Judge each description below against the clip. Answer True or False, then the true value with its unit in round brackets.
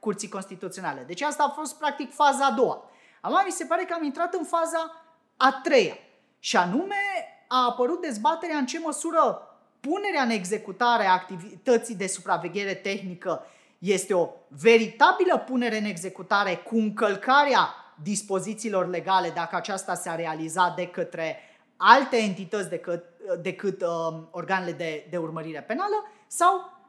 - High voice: True (215 Hz)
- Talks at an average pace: True (145 wpm)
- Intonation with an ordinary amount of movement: False (8.5 semitones)